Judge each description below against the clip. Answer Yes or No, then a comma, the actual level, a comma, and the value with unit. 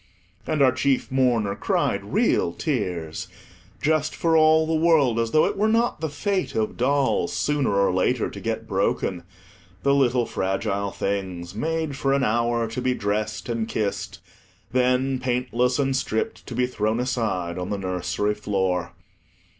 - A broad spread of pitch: Yes, wide, 5.7 semitones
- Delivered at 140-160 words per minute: Yes, average, 155 wpm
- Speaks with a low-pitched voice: Yes, low, 120 Hz